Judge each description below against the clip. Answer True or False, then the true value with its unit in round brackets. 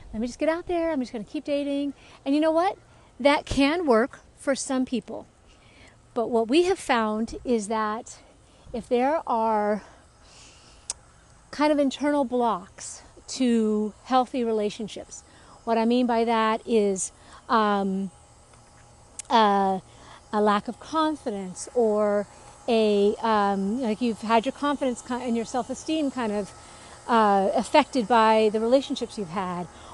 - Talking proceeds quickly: False (140 wpm)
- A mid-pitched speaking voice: False (230 Hz)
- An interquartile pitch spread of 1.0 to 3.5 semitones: False (4.0 semitones)